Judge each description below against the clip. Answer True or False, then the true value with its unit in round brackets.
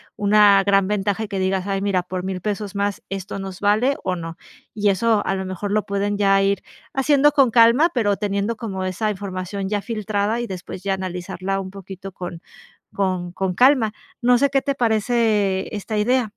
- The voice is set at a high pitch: True (200 Hz)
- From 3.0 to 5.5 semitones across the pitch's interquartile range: False (2.4 semitones)